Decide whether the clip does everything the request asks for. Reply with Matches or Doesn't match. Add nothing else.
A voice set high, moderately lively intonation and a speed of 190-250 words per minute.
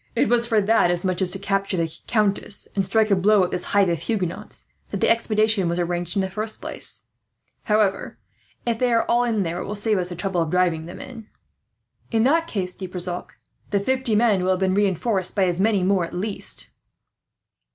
Matches